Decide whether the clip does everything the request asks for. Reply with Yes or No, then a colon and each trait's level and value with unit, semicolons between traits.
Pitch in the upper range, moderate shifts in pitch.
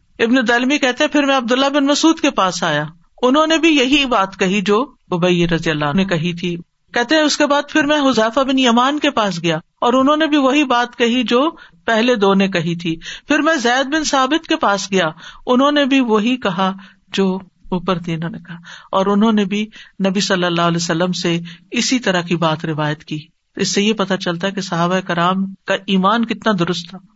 No: high, 205 Hz; wide, 6.7 semitones